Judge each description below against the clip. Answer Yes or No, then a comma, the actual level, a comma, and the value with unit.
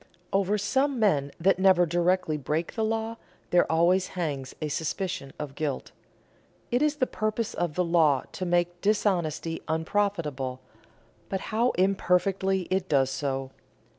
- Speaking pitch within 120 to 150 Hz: No, medium, 180 Hz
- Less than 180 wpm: Yes, average, 140 wpm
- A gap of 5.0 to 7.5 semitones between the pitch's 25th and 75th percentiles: No, average, 4.3 semitones